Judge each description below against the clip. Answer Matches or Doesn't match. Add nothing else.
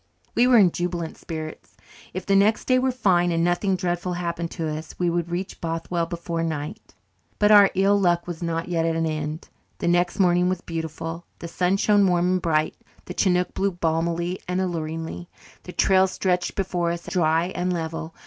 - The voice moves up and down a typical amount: Doesn't match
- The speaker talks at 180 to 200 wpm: Matches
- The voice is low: Doesn't match